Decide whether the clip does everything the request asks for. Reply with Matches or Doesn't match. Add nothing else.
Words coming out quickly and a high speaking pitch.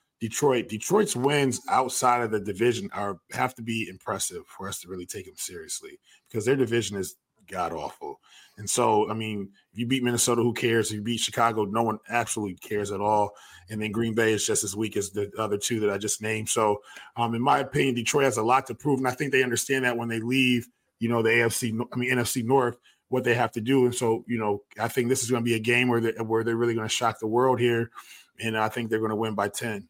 Doesn't match